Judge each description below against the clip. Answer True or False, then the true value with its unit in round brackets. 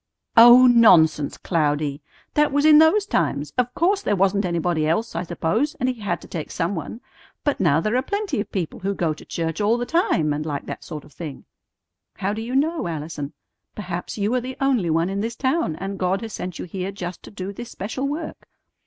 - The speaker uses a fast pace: True (220 wpm)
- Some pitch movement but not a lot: False (7.2 semitones)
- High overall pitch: True (195 Hz)